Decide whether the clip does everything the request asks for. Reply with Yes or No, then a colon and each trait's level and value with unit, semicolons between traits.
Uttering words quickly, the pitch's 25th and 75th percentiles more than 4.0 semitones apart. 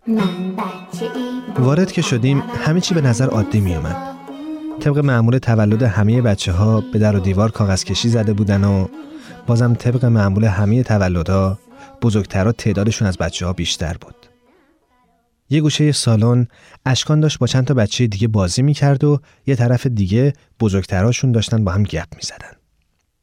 Yes: fast, 160 wpm; wide, 5.6 semitones